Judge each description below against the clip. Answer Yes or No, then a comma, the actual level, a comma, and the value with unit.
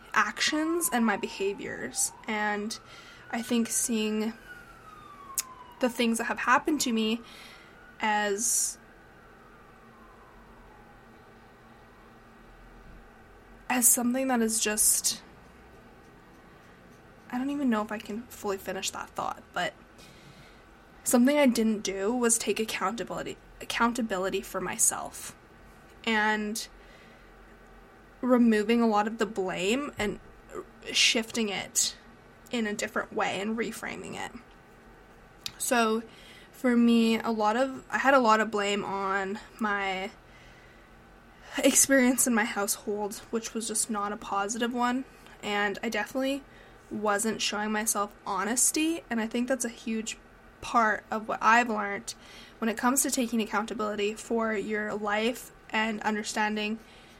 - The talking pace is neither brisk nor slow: No, slow, 120 wpm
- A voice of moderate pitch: No, high, 220 Hz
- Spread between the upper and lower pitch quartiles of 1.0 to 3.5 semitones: Yes, average, 2.7 semitones